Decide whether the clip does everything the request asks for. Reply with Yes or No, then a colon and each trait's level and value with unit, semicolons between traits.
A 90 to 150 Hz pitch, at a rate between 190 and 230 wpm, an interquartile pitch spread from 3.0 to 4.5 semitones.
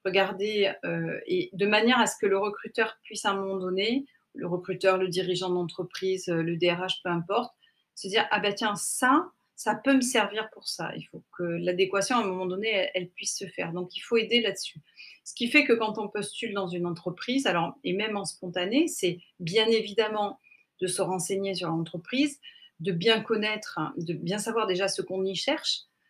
No: high, 195 Hz; average, 200 wpm; average, 3.3 semitones